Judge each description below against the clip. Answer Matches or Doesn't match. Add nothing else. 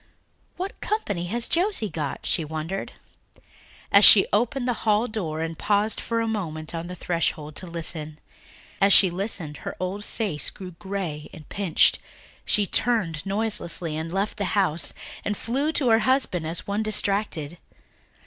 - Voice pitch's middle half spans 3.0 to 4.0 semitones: Doesn't match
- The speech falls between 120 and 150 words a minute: Doesn't match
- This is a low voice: Doesn't match